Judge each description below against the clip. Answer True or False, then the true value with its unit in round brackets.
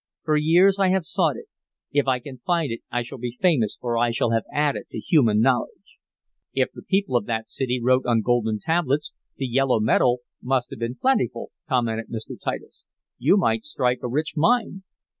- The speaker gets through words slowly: False (195 wpm)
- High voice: False (130 Hz)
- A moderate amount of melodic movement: True (4.5 semitones)